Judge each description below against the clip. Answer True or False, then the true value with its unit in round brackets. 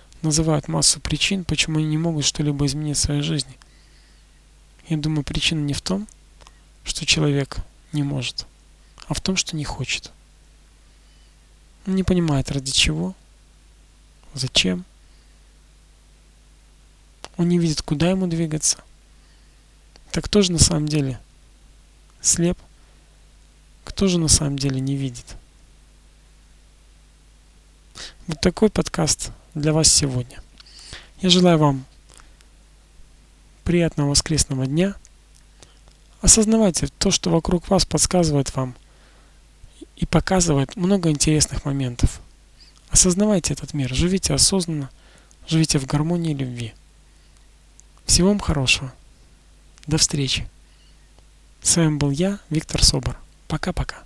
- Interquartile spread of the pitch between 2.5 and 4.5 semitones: False (5.5 semitones)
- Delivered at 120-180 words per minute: False (110 wpm)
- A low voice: False (145 Hz)